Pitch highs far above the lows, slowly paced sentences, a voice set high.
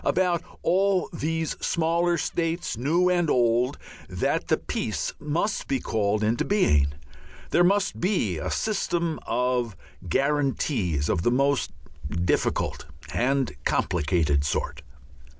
No: wide, 8.2 semitones; slow, 115 wpm; medium, 140 Hz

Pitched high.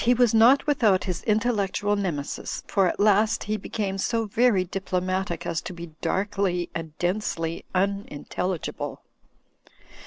Yes: high, 195 Hz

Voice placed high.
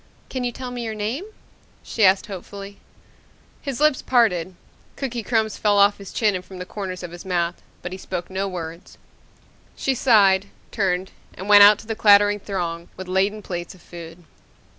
Yes: high, 200 Hz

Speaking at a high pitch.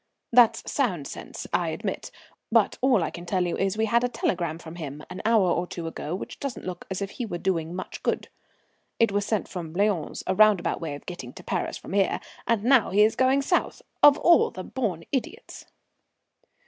Yes: high, 195 Hz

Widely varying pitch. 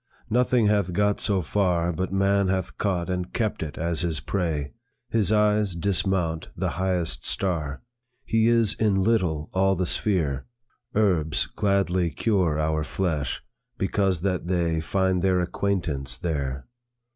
No: average, 3.5 semitones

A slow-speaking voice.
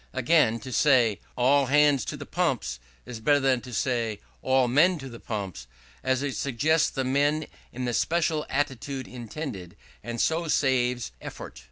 No: average, 165 wpm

